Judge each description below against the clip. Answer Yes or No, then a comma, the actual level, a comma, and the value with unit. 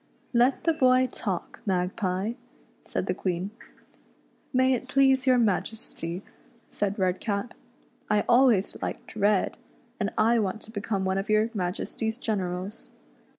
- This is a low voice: No, high, 210 Hz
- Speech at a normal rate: Yes, average, 145 wpm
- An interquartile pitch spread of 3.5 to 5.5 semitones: Yes, average, 3.9 semitones